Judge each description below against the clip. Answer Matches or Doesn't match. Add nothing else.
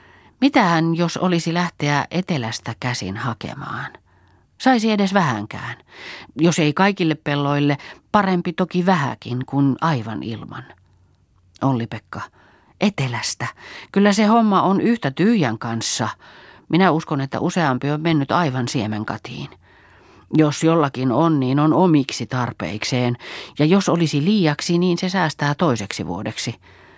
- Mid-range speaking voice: Matches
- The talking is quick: Doesn't match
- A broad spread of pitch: Matches